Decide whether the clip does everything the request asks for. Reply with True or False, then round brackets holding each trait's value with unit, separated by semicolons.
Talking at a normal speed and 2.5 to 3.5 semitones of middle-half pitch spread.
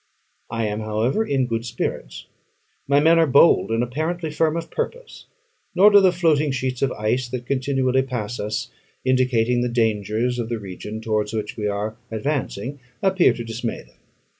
False (170 wpm; 4.5 semitones)